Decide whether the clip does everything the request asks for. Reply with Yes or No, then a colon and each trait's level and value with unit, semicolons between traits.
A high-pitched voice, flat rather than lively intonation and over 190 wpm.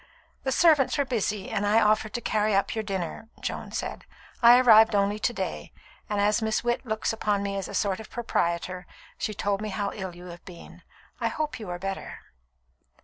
Yes: high, 210 Hz; narrow, 2.3 semitones; average, 200 wpm